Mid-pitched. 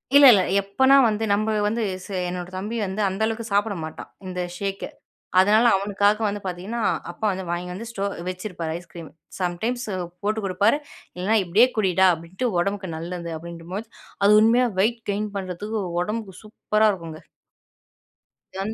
No: high, 200 Hz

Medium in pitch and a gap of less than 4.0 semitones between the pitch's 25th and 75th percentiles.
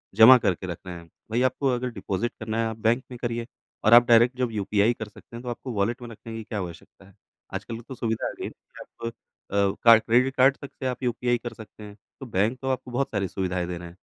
No: low, 115 Hz; average, 3.4 semitones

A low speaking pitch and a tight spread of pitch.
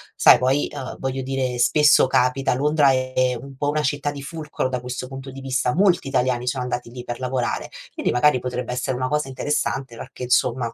Yes: low, 130 Hz; narrow, 1.7 semitones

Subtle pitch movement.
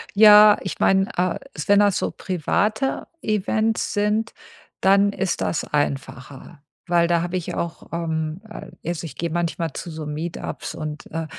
No: average, 4.1 semitones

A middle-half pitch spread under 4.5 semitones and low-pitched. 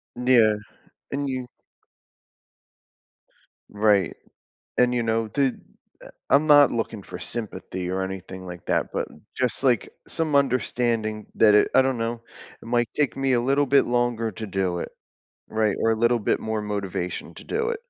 Yes: average, 3.6 semitones; low, 115 Hz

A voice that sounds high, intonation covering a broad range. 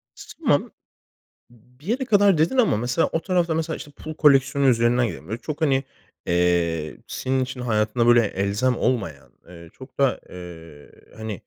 No: low, 125 Hz; wide, 6.8 semitones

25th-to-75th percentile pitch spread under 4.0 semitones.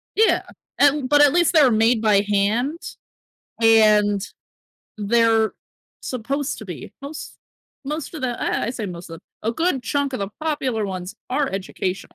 No: wide, 5.5 semitones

